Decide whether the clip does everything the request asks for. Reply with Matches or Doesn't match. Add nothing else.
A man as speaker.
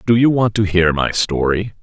Matches